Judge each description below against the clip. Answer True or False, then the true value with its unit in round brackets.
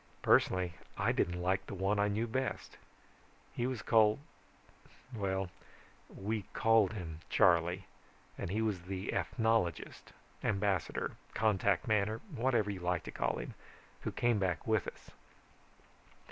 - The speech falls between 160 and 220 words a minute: False (135 wpm)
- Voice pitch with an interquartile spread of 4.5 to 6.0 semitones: False (3.2 semitones)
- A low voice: True (100 Hz)